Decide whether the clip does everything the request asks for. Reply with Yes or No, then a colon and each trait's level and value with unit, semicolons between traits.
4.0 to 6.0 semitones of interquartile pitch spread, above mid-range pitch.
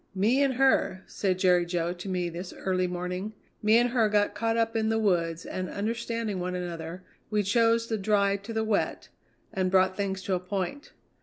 No: average, 3.5 semitones; high, 195 Hz